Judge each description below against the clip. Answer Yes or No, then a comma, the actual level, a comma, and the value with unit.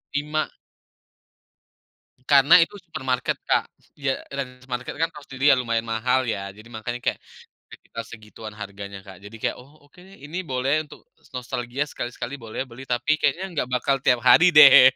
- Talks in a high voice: No, low, 130 Hz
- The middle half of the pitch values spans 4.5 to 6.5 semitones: No, average, 4.0 semitones